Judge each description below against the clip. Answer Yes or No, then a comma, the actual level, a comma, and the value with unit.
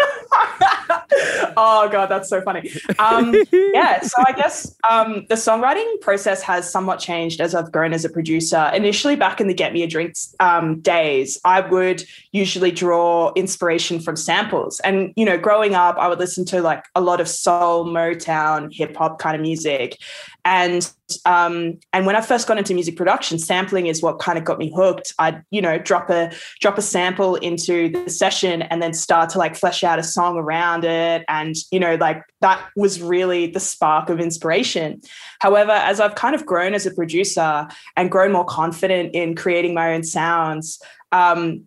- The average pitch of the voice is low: No, medium, 180 Hz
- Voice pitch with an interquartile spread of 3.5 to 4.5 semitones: No, average, 2.8 semitones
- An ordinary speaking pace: Yes, average, 185 wpm